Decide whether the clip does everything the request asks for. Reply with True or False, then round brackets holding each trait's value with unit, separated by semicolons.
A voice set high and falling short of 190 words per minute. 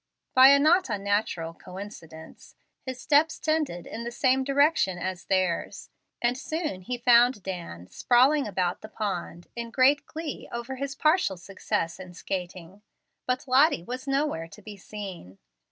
True (230 Hz; 150 wpm)